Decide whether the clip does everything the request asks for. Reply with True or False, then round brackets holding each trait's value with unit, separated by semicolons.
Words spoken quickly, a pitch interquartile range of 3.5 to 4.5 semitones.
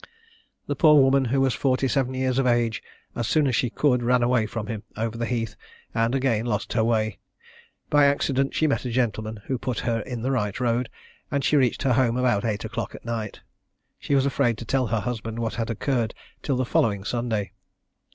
False (210 wpm; 2.6 semitones)